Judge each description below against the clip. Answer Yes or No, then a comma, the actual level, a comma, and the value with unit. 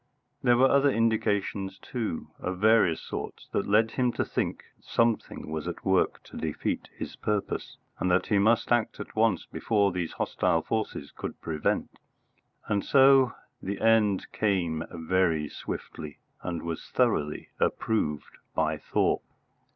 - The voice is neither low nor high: No, low, 100 Hz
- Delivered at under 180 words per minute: Yes, average, 145 wpm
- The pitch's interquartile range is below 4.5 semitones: No, average, 5.1 semitones